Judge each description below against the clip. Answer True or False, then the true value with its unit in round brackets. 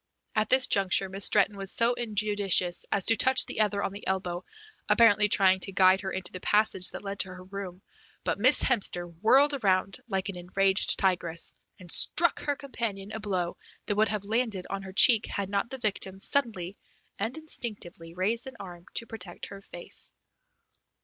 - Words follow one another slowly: False (185 wpm)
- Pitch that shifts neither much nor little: True (3.0 semitones)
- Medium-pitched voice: False (200 Hz)